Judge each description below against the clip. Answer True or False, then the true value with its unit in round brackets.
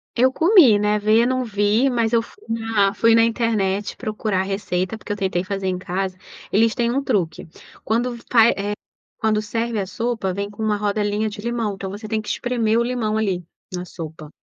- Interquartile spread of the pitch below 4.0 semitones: True (2.6 semitones)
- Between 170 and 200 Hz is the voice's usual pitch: False (215 Hz)